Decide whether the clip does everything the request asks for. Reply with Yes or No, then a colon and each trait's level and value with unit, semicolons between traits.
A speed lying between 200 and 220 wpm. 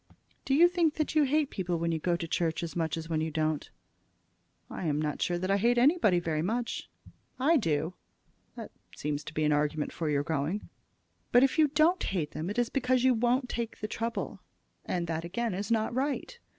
Yes: fast, 205 wpm